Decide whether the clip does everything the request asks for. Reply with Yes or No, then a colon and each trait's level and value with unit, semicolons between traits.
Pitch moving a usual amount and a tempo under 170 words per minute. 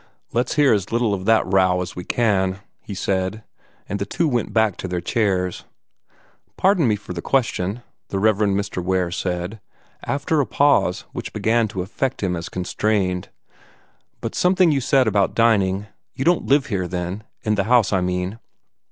No: average, 4.2 semitones; average, 180 wpm